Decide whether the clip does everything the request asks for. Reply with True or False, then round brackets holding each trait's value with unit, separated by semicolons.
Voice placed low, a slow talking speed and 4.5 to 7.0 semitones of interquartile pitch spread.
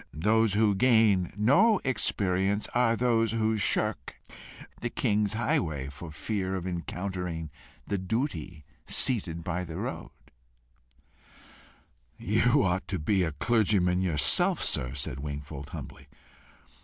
True (95 Hz; 120 wpm; 5.1 semitones)